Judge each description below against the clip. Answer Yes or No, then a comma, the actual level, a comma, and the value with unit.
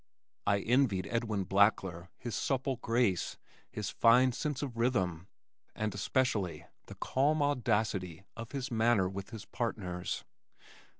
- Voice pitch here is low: Yes, low, 110 Hz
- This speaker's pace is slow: Yes, slow, 125 wpm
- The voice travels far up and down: No, average, 4.3 semitones